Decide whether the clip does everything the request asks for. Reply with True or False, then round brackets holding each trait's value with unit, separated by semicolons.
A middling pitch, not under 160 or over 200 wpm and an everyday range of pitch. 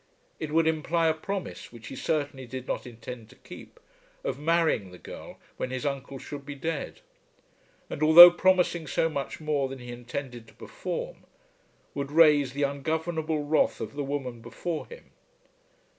True (145 Hz; 165 wpm; 3.7 semitones)